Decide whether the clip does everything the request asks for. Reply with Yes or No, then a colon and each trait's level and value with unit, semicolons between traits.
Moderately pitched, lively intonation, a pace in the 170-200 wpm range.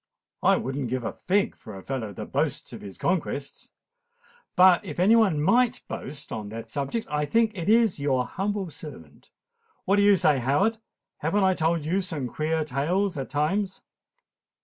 Yes: medium, 160 Hz; wide, 6.2 semitones; average, 180 wpm